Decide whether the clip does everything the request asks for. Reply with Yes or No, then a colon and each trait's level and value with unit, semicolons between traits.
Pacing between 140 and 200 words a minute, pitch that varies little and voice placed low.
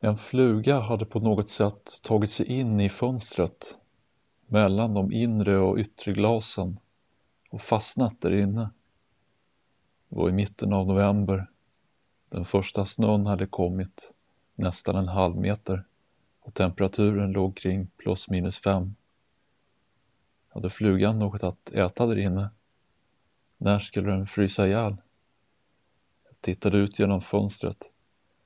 No: slow, 125 wpm; narrow, 1.9 semitones; low, 100 Hz